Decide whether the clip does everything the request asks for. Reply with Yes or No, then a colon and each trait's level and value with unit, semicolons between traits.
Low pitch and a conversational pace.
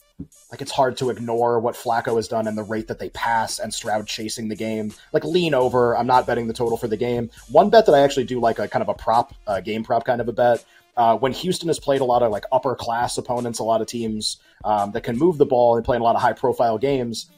No: low, 120 Hz; fast, 280 wpm